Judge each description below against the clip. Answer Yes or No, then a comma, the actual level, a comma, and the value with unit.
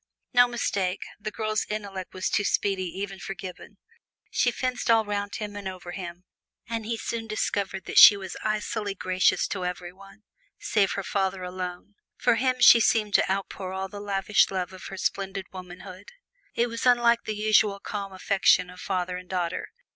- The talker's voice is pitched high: Yes, high, 200 Hz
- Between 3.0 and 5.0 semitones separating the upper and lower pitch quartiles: No, narrow, 2.5 semitones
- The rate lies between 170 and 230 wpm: Yes, average, 180 wpm